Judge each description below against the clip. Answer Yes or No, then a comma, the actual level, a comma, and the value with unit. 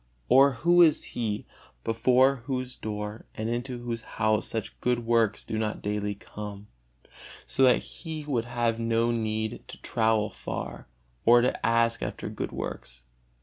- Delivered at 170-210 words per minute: No, average, 150 wpm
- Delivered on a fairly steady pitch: Yes, narrow, 2.3 semitones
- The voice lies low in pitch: Yes, low, 115 Hz